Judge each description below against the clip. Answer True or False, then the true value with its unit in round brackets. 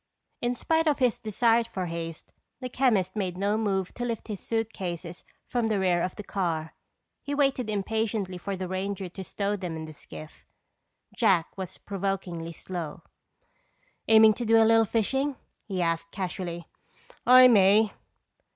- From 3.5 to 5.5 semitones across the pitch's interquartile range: True (3.9 semitones)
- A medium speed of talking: True (160 wpm)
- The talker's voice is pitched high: True (200 Hz)